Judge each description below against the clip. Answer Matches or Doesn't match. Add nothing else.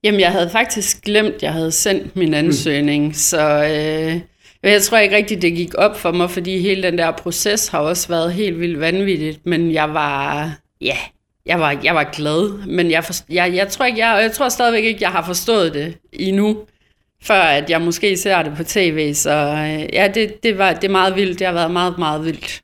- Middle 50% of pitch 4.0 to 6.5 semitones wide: Matches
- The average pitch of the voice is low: Doesn't match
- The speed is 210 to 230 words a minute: Matches